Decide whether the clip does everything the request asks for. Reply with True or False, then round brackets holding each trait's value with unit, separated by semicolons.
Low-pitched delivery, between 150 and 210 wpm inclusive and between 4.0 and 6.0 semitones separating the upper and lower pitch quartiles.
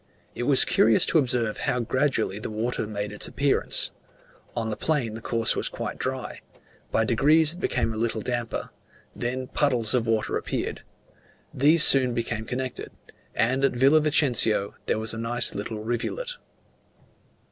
False (120 Hz; 160 wpm; 3.3 semitones)